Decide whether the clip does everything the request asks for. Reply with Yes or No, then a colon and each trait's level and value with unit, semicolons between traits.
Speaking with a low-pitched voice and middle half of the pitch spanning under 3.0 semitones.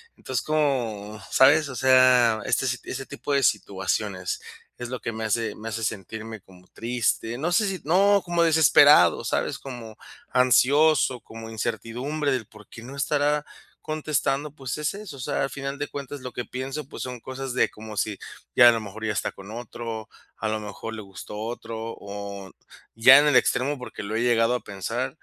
No: low, 125 Hz; average, 4.1 semitones